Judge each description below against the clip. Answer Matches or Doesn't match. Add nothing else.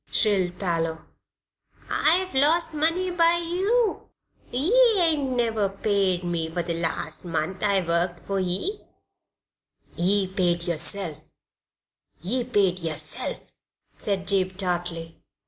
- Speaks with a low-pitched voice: Doesn't match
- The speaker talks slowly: Matches